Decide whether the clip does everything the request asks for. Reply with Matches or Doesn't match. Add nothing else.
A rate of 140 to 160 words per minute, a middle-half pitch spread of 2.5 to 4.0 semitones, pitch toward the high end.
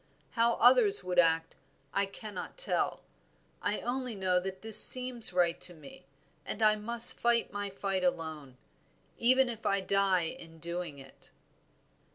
Doesn't match